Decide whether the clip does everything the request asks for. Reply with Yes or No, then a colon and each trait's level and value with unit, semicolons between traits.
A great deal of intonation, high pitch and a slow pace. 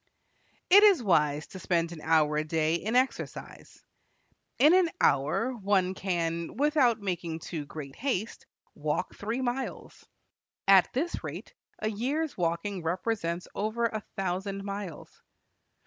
Yes: wide, 6.0 semitones; high, 195 Hz; slow, 130 wpm